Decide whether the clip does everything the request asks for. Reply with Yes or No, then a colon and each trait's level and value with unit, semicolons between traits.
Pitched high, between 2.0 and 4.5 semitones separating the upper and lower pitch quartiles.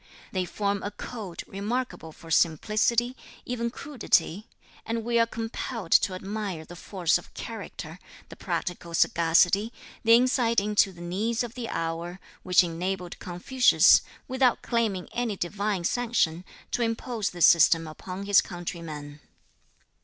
No: high, 200 Hz; average, 4.9 semitones